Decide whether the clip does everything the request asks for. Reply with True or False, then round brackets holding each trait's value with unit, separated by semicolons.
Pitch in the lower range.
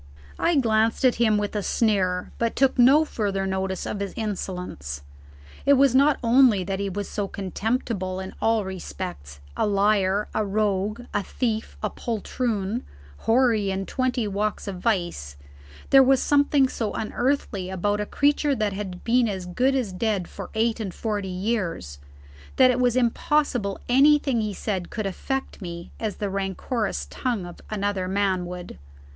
False (210 Hz)